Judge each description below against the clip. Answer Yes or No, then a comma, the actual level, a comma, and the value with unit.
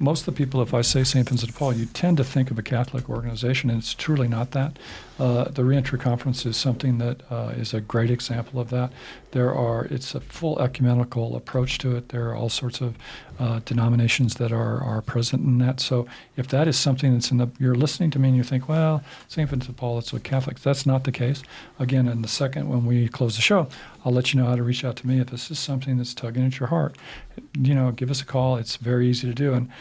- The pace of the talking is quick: Yes, fast, 255 wpm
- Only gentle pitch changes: Yes, narrow, 1.7 semitones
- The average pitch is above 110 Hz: Yes, low, 125 Hz